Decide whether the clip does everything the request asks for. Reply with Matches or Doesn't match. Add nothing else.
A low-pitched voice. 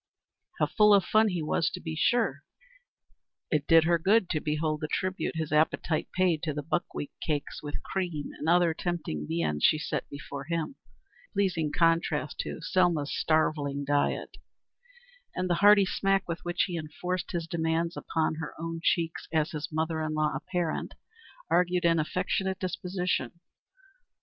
Doesn't match